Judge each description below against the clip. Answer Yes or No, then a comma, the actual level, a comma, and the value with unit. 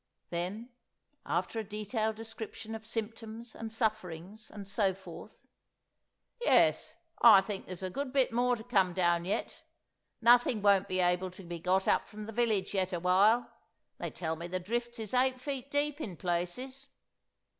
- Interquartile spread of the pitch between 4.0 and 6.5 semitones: Yes, average, 4.3 semitones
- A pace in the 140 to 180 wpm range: Yes, average, 160 wpm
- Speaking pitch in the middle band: No, high, 215 Hz